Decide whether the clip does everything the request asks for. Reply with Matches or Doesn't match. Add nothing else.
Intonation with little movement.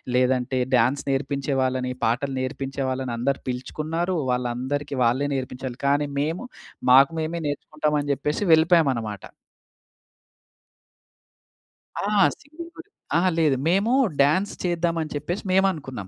Doesn't match